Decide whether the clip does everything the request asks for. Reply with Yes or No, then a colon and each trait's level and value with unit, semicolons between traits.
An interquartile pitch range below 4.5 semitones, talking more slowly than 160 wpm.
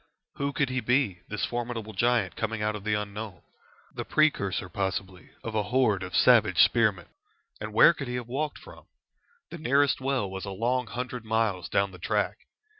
No: average, 4.1 semitones; average, 185 wpm